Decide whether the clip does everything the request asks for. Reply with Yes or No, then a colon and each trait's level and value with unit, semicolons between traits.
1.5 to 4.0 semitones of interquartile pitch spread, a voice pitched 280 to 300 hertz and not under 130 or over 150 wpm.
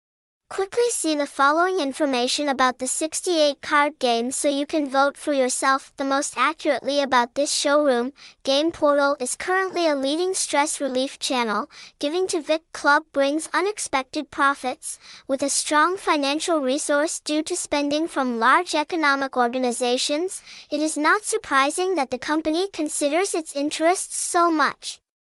Yes: average, 2.9 semitones; very high, 295 Hz; average, 145 wpm